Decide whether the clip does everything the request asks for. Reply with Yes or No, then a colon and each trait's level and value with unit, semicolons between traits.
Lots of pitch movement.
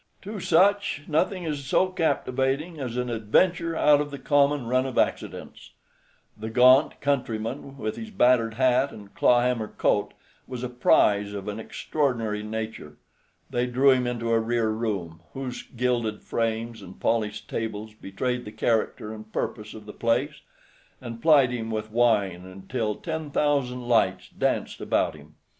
No: average, 4.1 semitones